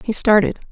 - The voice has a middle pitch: No, high, 210 Hz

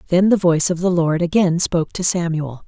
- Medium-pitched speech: Yes, medium, 170 Hz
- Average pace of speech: No, fast, 225 wpm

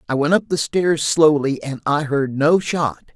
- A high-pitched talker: No, medium, 150 Hz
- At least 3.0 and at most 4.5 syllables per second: Yes, 4.4 syllables/s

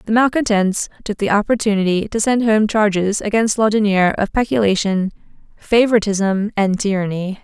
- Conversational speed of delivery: No, slow, 130 wpm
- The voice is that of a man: No, female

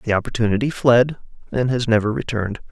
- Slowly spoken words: No, average, 155 wpm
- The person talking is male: Yes, male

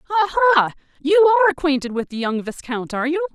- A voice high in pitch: Yes, very high, 315 Hz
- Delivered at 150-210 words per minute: Yes, average, 195 wpm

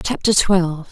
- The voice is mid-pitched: Yes, medium, 180 Hz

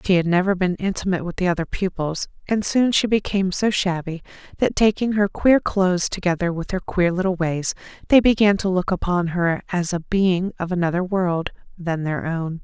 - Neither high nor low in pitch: Yes, medium, 180 Hz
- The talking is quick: No, average, 195 wpm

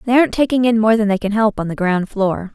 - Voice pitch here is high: Yes, high, 215 Hz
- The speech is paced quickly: Yes, fast, 305 wpm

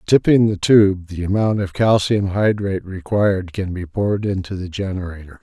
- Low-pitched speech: Yes, very low, 95 Hz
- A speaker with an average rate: Yes, average, 175 wpm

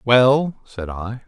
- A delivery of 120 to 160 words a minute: Yes, average, 140 wpm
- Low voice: Yes, low, 120 Hz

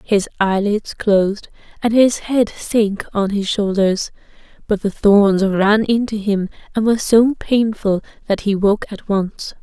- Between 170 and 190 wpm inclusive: No, average, 155 wpm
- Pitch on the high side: Yes, high, 210 Hz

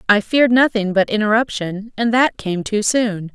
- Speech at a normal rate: Yes, average, 180 wpm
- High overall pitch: Yes, high, 215 Hz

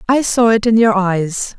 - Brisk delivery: Yes, fast, 225 wpm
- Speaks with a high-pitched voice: Yes, high, 215 Hz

